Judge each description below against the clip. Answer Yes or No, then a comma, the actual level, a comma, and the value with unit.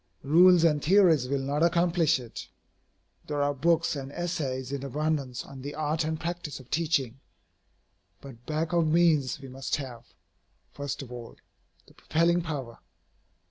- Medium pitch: Yes, medium, 150 Hz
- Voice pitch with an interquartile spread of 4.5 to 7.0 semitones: No, average, 3.7 semitones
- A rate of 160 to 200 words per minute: No, average, 150 wpm